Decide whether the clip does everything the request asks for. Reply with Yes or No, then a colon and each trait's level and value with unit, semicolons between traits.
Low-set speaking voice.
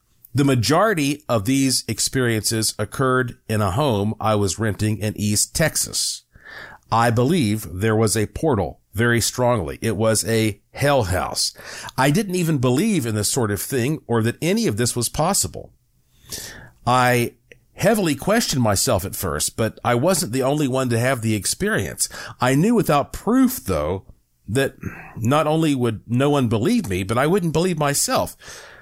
Yes: low, 120 Hz